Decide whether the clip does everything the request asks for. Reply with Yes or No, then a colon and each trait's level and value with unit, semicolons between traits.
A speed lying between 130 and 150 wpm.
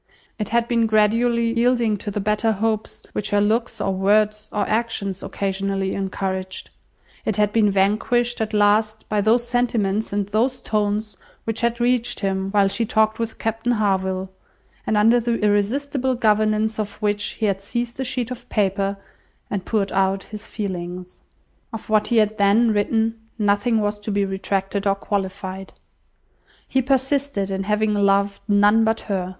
No: average, 165 wpm